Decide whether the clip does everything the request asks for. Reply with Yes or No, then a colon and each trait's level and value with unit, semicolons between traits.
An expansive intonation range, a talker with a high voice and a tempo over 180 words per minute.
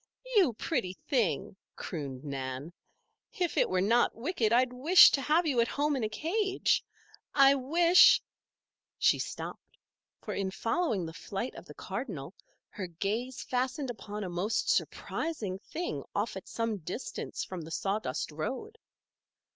No: wide, 7.7 semitones; high, 230 Hz; average, 150 wpm